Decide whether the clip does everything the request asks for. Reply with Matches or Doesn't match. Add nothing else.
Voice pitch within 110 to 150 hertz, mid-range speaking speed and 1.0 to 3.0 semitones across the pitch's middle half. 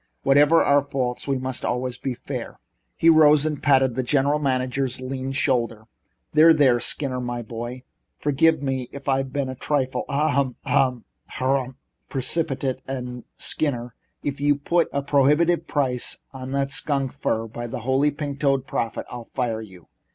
Matches